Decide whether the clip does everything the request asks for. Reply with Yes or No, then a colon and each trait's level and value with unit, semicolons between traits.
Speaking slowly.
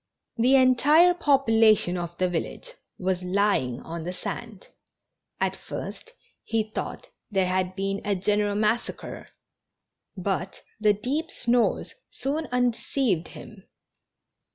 Yes: slow, 115 wpm